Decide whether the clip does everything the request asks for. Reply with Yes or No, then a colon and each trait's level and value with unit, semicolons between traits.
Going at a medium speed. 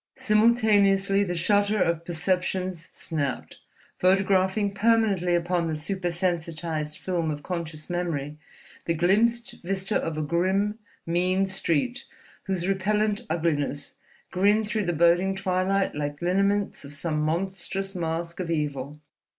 No: slow, 125 wpm